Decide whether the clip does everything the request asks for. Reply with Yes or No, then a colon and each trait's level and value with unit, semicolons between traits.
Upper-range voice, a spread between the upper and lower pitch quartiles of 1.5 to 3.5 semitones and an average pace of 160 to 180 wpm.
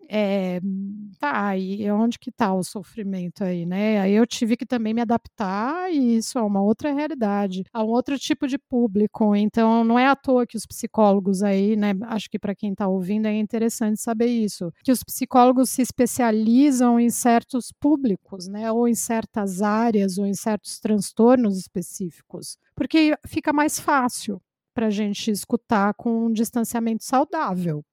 Yes: high, 220 Hz; average, 3.2 semitones; average, 170 wpm